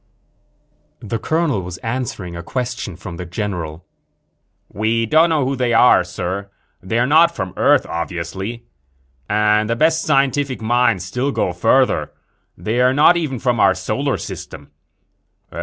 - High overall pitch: No, low, 115 Hz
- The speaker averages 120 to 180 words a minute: Yes, average, 140 wpm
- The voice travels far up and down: Yes, wide, 5.9 semitones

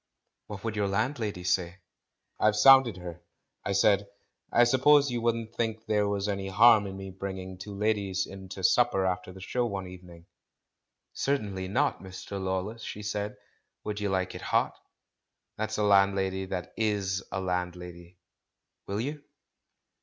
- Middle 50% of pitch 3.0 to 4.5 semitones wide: No, narrow, 2.6 semitones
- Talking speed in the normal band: Yes, average, 160 wpm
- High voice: No, low, 100 Hz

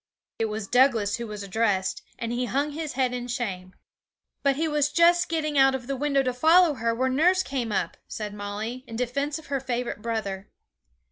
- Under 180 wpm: No, average, 200 wpm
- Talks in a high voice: Yes, very high, 250 Hz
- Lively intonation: No, average, 4.4 semitones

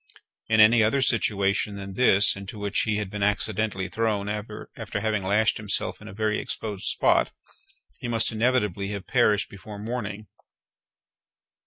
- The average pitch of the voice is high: No, low, 105 Hz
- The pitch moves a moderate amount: No, narrow, 1.6 semitones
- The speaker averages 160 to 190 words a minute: No, average, 150 wpm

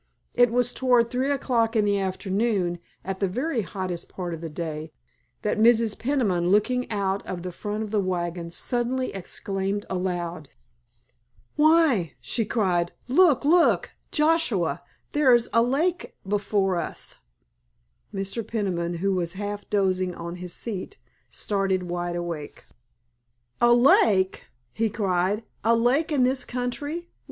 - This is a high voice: Yes, high, 205 Hz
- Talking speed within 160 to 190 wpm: No, average, 140 wpm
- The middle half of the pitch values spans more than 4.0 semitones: Yes, average, 5.2 semitones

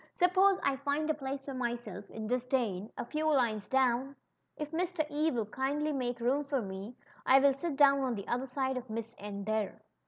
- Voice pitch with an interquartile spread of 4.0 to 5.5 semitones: No, average, 3.6 semitones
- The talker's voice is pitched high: Yes, very high, 265 Hz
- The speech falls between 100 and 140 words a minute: No, fast, 205 wpm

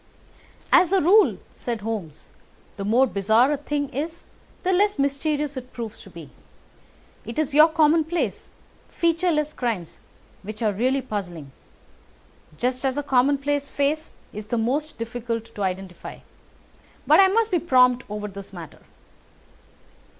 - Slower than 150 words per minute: Yes, average, 140 wpm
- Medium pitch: No, very high, 260 Hz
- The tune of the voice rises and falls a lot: Yes, wide, 5.9 semitones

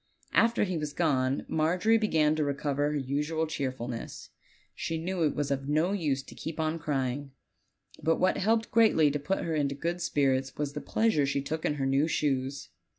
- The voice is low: No, medium, 150 Hz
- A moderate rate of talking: Yes, average, 195 wpm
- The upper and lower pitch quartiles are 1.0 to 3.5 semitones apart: Yes, average, 3.0 semitones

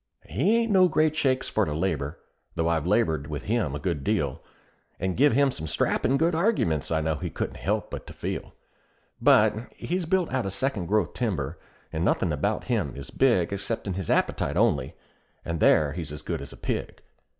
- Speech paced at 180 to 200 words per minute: Yes, average, 195 wpm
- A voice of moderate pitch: No, very low, 95 Hz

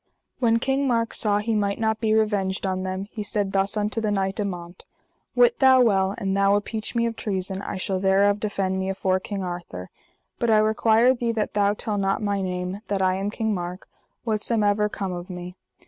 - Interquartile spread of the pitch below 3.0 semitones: Yes, narrow, 2.4 semitones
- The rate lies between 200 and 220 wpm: Yes, fast, 205 wpm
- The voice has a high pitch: Yes, high, 205 Hz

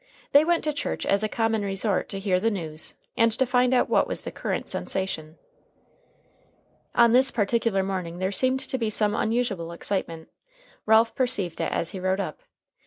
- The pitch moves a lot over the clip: No, average, 4.2 semitones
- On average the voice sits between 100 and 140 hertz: No, high, 210 Hz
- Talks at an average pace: Yes, average, 180 wpm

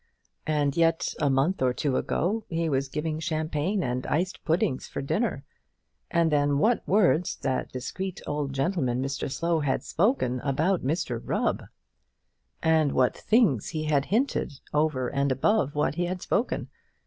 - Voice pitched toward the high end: No, medium, 155 Hz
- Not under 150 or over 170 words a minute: Yes, average, 155 wpm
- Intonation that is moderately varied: Yes, average, 4.2 semitones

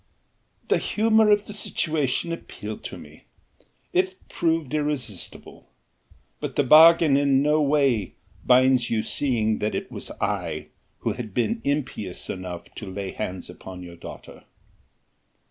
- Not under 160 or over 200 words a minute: No, slow, 135 wpm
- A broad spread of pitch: Yes, wide, 6.7 semitones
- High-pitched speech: No, low, 135 Hz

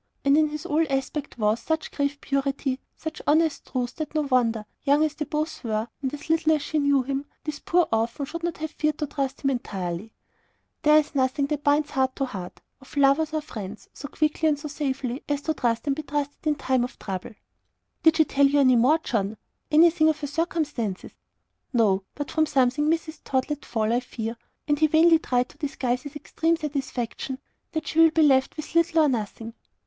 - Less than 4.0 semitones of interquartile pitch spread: Yes, average, 3.4 semitones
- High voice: Yes, very high, 285 Hz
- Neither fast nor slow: No, fast, 210 wpm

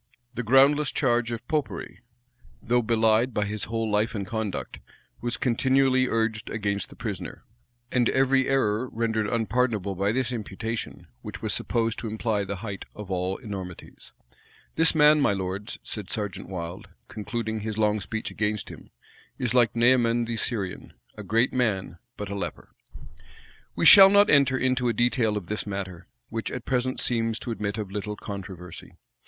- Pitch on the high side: No, low, 110 Hz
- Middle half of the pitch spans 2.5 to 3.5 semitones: Yes, average, 3.2 semitones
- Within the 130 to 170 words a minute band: Yes, average, 165 wpm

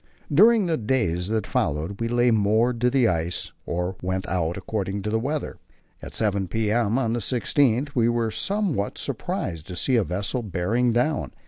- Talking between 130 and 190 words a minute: Yes, average, 180 wpm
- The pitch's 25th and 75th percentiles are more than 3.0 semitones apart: Yes, average, 4.5 semitones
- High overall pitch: No, low, 110 Hz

